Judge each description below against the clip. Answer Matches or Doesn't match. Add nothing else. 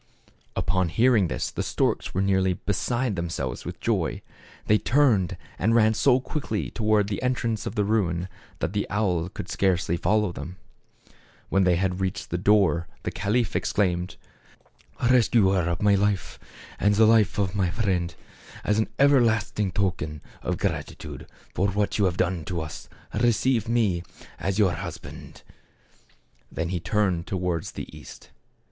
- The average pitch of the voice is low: Matches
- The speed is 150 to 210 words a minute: Matches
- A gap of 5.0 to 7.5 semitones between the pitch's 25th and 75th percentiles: Doesn't match